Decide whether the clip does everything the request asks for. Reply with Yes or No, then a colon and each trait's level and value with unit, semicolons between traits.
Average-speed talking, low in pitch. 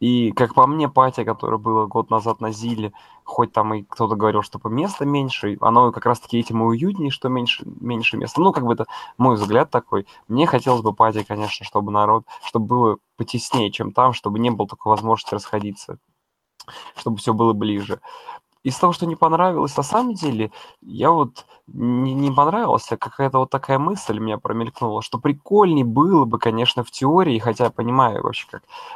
No: fast, 190 wpm; low, 120 Hz